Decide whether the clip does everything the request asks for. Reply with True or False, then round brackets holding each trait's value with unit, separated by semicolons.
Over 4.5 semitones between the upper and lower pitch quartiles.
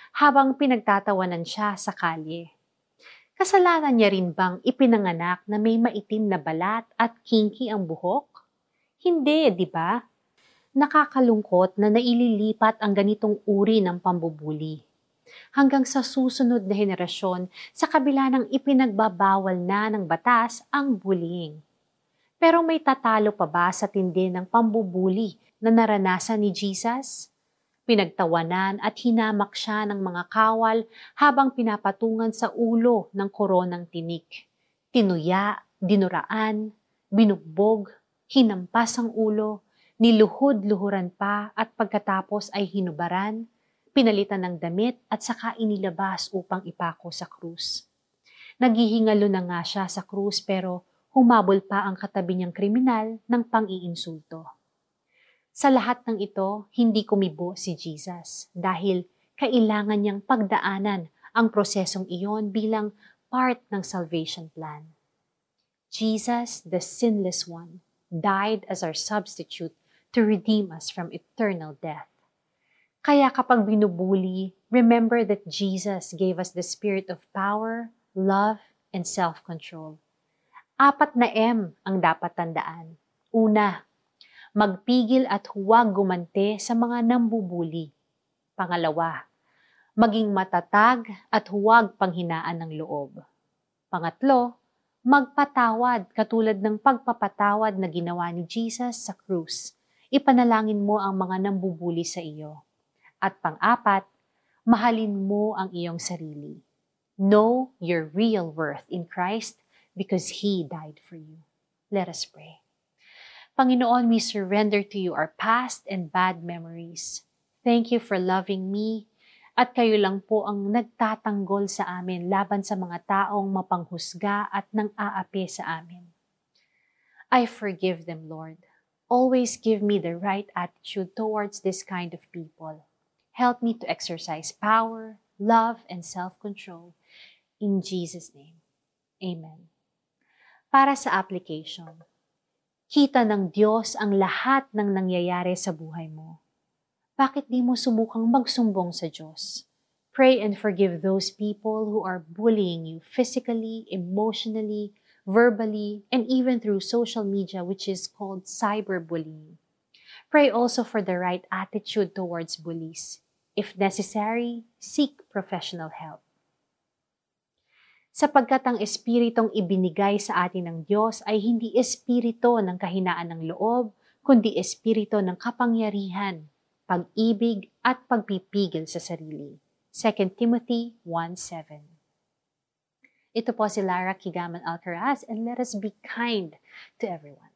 False (4.2 semitones)